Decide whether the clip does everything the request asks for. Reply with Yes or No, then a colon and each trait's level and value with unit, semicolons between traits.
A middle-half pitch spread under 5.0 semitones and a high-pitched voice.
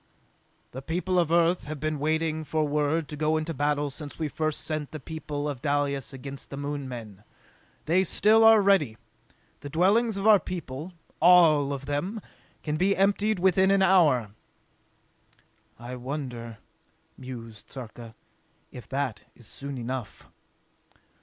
No: average, 4.4 semitones; medium, 150 Hz